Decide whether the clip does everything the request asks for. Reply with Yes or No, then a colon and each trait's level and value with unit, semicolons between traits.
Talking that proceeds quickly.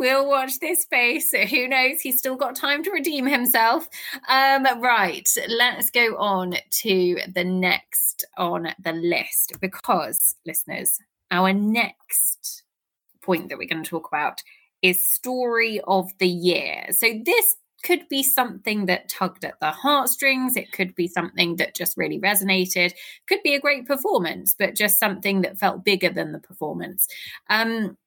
No: average, 155 wpm